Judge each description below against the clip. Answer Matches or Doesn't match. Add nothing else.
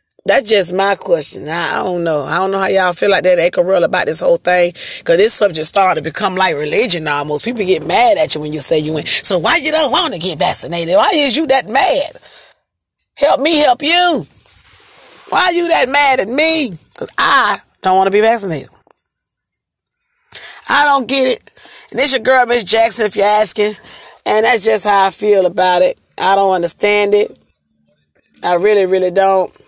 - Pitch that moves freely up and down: Matches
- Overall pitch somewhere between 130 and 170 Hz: Doesn't match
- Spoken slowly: Doesn't match